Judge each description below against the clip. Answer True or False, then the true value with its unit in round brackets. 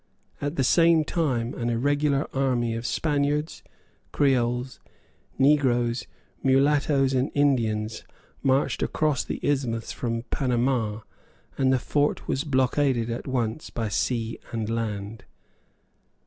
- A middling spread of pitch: True (3.5 semitones)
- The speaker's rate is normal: False (115 wpm)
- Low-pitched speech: True (130 Hz)